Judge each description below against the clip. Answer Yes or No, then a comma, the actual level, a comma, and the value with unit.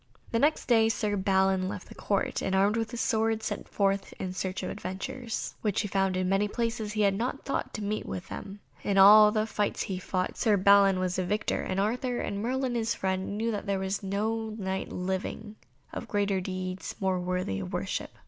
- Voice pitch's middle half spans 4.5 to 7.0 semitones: No, narrow, 2.5 semitones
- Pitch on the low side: No, high, 200 Hz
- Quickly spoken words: Yes, fast, 220 wpm